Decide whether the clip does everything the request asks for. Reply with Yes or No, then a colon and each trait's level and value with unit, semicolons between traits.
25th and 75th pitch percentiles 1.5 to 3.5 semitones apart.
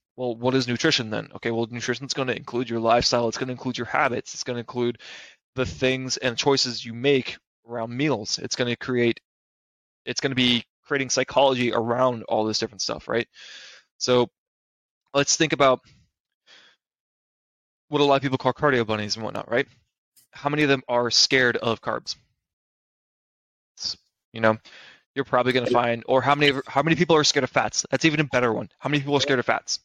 Yes: average, 2.9 semitones